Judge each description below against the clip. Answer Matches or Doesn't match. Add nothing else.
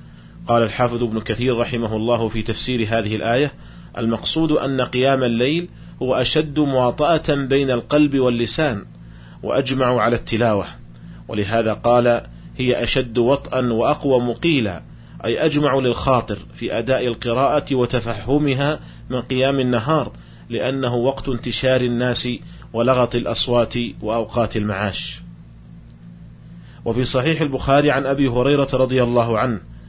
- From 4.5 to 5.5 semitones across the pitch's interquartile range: Doesn't match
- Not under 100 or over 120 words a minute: Matches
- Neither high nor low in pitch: Doesn't match